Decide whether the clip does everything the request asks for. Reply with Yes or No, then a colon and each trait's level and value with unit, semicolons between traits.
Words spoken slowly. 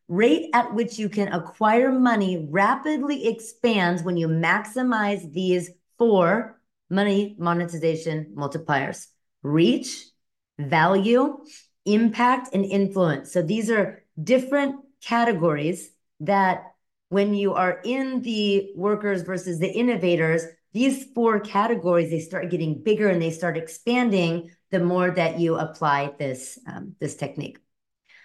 Yes: slow, 120 wpm